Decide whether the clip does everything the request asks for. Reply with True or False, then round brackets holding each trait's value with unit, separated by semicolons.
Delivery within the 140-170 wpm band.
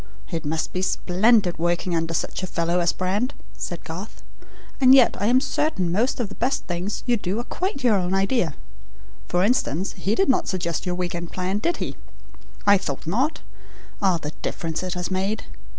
False (195 wpm)